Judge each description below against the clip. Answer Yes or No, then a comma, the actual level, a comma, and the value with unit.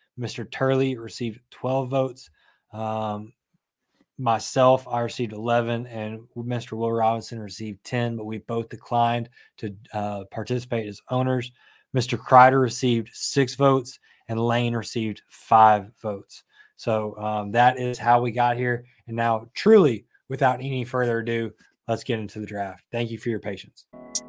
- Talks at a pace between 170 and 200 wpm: No, average, 150 wpm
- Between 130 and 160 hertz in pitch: No, low, 120 Hz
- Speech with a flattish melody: Yes, narrow, 2.2 semitones